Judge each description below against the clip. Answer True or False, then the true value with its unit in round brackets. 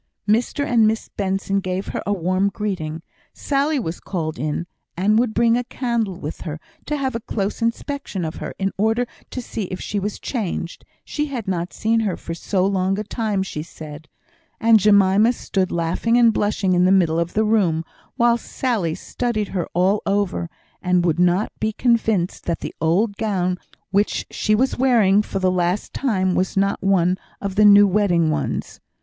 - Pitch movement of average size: True (3.7 semitones)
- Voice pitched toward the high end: True (200 Hz)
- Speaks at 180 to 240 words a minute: True (185 wpm)